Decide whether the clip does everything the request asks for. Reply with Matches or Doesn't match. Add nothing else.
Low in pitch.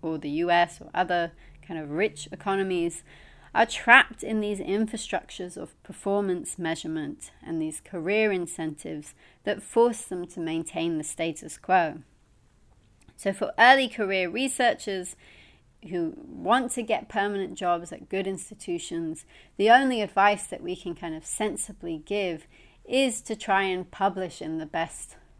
Doesn't match